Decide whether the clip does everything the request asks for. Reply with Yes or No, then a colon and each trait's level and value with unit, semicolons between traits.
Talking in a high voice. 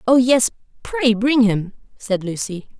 Yes: high, 230 Hz